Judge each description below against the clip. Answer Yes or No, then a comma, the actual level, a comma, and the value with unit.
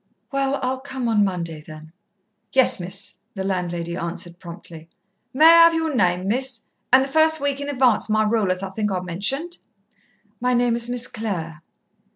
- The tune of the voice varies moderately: No, wide, 6.7 semitones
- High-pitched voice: Yes, high, 220 Hz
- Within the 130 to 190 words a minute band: Yes, average, 180 wpm